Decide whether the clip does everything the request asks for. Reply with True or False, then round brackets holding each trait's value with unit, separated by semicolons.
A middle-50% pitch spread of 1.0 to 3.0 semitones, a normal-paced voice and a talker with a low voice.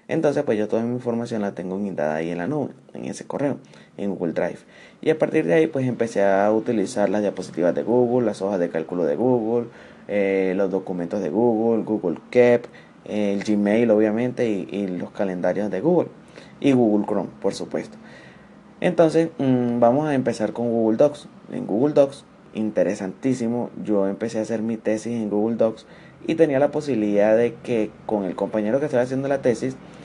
False (3.6 semitones; 190 wpm; 115 Hz)